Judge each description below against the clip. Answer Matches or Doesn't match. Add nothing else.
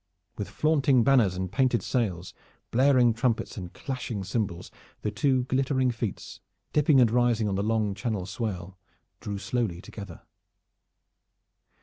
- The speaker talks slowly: Matches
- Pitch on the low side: Matches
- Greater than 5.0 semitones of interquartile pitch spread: Doesn't match